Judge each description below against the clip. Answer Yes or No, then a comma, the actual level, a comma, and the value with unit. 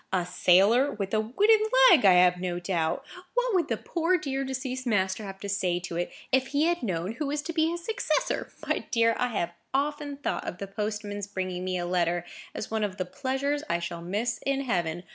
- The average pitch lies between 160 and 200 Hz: No, high, 210 Hz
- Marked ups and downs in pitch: Yes, wide, 7.4 semitones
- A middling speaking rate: No, fast, 210 wpm